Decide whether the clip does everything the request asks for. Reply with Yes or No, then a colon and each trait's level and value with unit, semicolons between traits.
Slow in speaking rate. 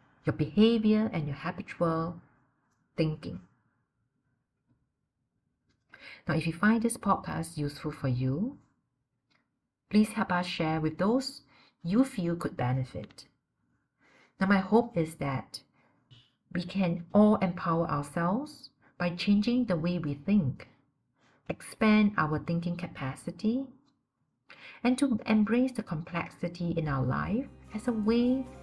Yes: slow, 115 wpm